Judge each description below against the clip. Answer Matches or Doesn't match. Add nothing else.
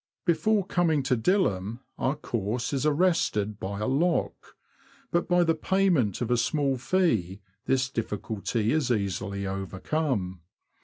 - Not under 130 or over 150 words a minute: Matches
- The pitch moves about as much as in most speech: Doesn't match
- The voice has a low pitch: Matches